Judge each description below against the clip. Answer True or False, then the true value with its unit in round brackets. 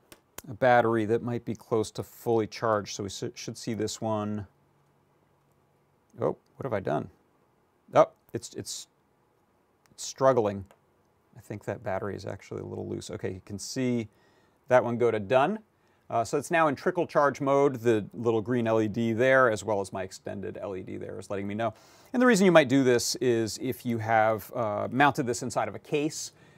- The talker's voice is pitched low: True (115 Hz)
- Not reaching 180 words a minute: False (190 wpm)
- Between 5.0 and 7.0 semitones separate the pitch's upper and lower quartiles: False (3.5 semitones)